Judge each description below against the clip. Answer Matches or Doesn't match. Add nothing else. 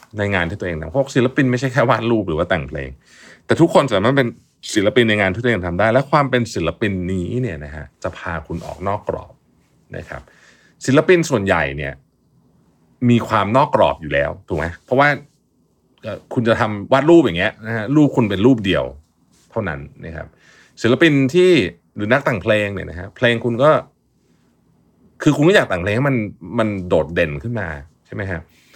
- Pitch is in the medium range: Doesn't match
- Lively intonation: Matches